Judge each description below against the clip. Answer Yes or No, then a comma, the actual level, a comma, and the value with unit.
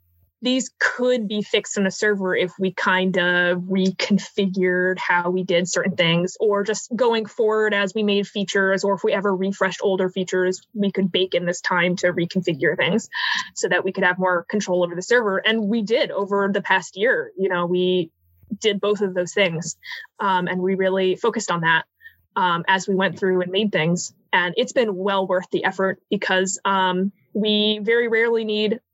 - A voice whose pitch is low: No, high, 190 Hz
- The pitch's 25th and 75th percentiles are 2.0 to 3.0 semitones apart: Yes, narrow, 2.6 semitones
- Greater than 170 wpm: Yes, average, 195 wpm